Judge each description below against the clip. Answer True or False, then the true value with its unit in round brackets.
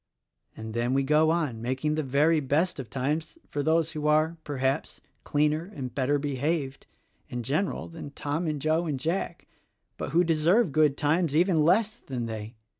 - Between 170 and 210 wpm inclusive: True (175 wpm)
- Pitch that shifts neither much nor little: True (3.3 semitones)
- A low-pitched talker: False (150 Hz)